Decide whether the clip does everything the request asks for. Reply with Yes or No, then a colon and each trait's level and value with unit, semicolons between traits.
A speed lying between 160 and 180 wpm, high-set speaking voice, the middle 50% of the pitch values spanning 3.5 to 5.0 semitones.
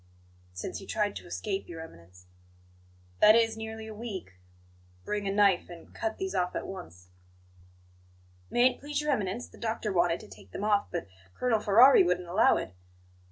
Yes: average, 175 wpm; high, 200 Hz; average, 4.1 semitones